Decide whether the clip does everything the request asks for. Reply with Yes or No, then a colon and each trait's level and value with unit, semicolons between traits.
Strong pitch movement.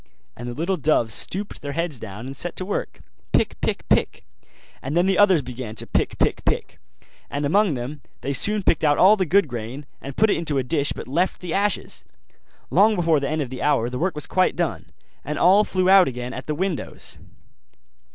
Yes: wide, 5.8 semitones